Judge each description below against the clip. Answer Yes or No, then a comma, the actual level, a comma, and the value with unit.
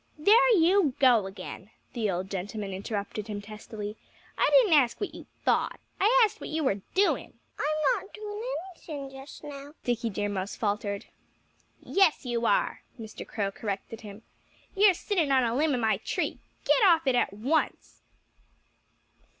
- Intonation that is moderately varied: No, wide, 7.8 semitones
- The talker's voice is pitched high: Yes, very high, 255 Hz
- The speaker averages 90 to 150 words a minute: No, average, 165 wpm